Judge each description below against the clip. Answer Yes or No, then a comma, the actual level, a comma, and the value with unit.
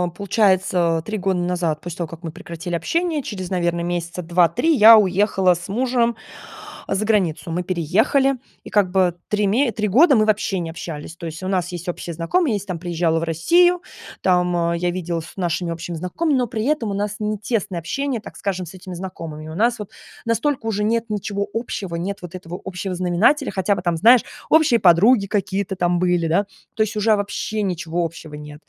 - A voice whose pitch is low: No, medium, 185 Hz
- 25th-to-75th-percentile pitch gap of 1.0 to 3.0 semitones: No, average, 3.9 semitones